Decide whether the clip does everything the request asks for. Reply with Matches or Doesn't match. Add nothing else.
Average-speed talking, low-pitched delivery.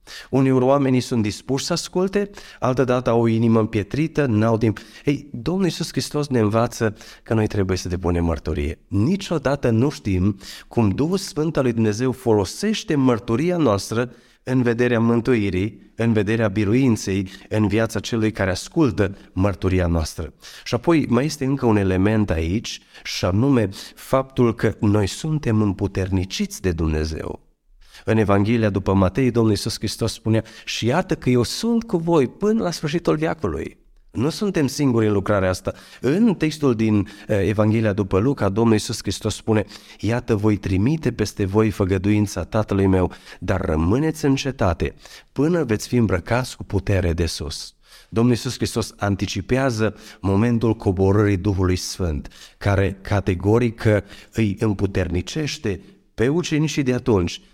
Matches